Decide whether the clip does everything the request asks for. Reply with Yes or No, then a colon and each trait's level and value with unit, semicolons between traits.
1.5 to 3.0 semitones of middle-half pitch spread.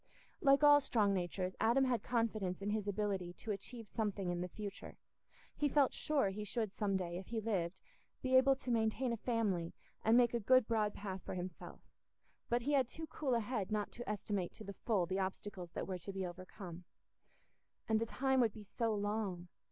No: average, 3.9 semitones